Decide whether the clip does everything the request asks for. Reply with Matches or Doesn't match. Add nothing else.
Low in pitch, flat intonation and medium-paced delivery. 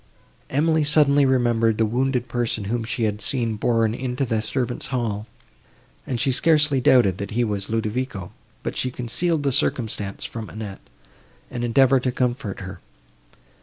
Doesn't match